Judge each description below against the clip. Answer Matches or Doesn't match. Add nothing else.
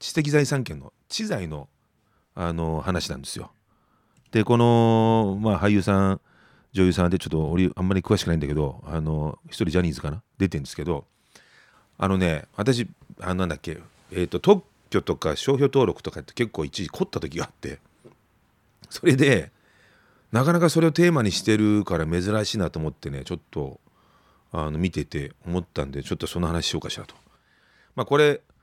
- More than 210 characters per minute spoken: Matches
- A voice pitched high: Doesn't match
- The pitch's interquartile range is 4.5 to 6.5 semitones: Matches